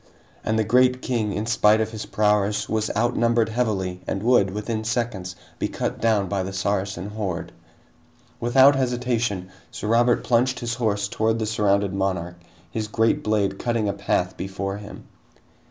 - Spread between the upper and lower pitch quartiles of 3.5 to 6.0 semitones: No, average, 2.8 semitones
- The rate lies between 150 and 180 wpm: Yes, average, 160 wpm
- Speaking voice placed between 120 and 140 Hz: No, low, 110 Hz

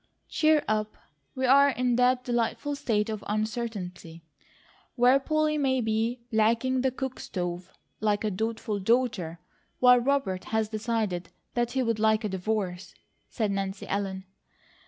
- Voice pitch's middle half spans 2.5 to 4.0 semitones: Yes, average, 3.7 semitones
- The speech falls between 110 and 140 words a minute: Yes, slow, 135 wpm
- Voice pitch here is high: Yes, high, 220 Hz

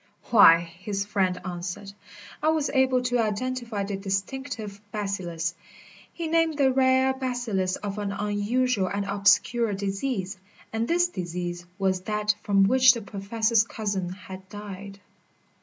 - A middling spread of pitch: Yes, average, 4.4 semitones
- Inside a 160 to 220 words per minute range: No, average, 140 wpm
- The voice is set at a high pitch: Yes, high, 205 Hz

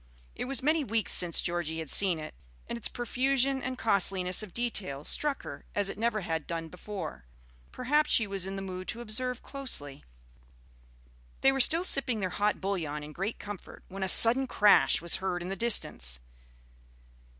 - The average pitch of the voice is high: Yes, high, 200 Hz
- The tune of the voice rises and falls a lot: Yes, wide, 5.7 semitones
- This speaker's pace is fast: No, average, 180 wpm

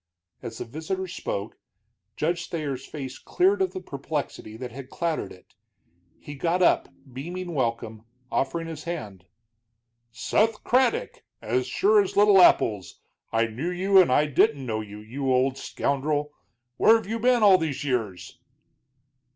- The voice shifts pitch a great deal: Yes, wide, 6.7 semitones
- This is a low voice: No, medium, 145 Hz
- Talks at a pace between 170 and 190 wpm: No, average, 150 wpm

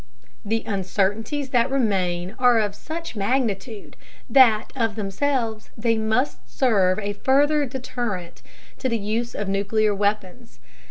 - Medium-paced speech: No, slow, 130 wpm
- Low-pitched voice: No, high, 220 Hz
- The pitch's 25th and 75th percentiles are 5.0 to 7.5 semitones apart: No, average, 3.9 semitones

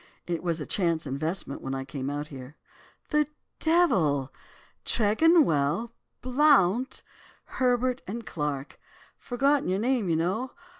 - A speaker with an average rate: No, slow, 120 wpm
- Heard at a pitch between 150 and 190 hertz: Yes, medium, 185 Hz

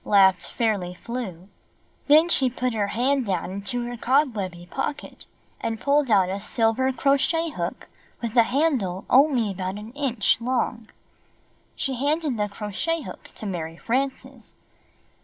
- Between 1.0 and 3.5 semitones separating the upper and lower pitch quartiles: No, average, 5.3 semitones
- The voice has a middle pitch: No, high, 235 Hz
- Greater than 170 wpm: No, average, 140 wpm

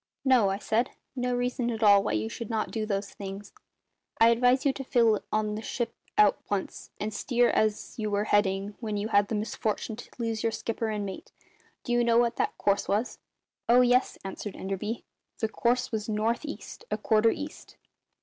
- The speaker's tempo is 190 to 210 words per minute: Yes, average, 200 wpm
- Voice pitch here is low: No, high, 220 Hz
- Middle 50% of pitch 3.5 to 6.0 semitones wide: No, narrow, 2.6 semitones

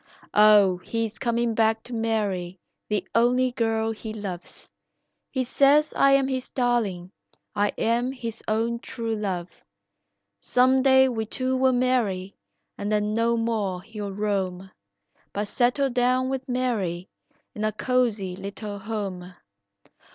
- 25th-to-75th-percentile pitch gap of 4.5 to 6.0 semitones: No, average, 3.7 semitones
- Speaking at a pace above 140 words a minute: No, slow, 135 wpm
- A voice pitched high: Yes, high, 225 Hz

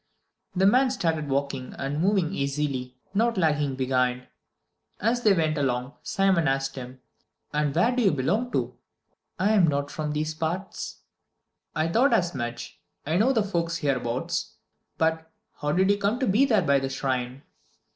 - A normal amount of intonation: No, wide, 6.2 semitones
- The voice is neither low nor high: Yes, medium, 155 Hz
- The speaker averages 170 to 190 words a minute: No, average, 160 wpm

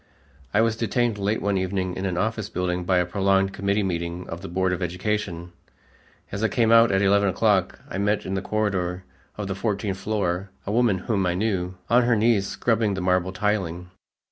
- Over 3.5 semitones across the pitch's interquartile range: No, narrow, 2.6 semitones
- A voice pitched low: Yes, very low, 95 Hz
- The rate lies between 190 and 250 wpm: Yes, average, 200 wpm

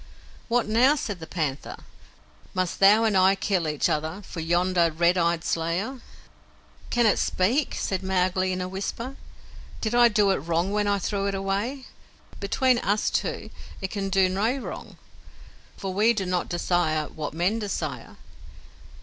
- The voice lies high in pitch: Yes, high, 195 Hz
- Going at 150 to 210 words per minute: Yes, average, 165 wpm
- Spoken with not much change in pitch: No, average, 3.5 semitones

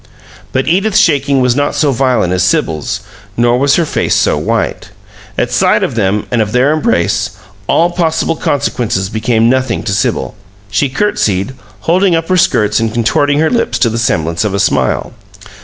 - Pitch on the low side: Yes, low, 125 Hz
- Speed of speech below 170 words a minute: No, average, 175 wpm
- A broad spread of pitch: Yes, wide, 6.1 semitones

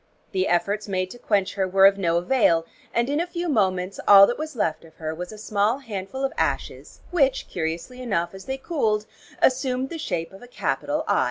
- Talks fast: Yes, fast, 210 wpm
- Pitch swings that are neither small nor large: No, wide, 6.1 semitones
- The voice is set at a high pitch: Yes, high, 205 Hz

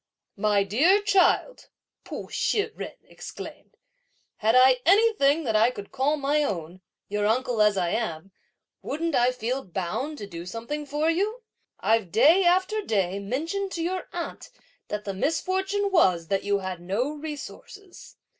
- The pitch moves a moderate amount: No, wide, 8.9 semitones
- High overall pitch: Yes, very high, 260 Hz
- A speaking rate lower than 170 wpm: Yes, average, 155 wpm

